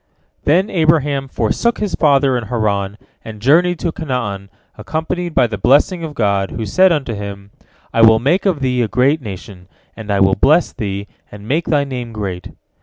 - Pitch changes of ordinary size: No, wide, 7.1 semitones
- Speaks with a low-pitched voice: Yes, low, 125 Hz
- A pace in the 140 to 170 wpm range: No, average, 185 wpm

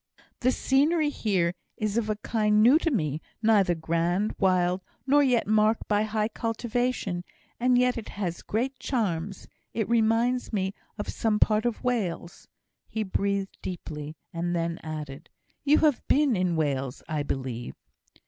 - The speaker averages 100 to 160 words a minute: Yes, average, 150 wpm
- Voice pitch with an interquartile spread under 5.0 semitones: No, wide, 5.5 semitones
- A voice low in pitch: No, high, 210 Hz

